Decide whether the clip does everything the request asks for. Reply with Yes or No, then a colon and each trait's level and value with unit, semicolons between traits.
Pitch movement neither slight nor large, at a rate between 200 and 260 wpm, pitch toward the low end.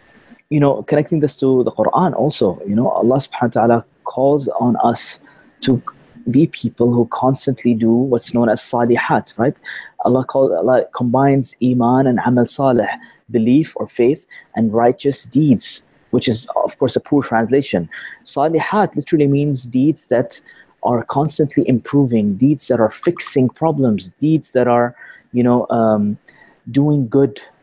No: average, 3.0 semitones; average, 150 wpm; low, 130 Hz